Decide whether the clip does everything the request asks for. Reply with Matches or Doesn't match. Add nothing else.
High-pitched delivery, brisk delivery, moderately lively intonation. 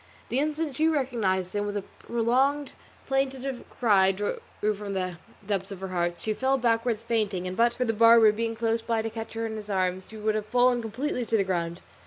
Matches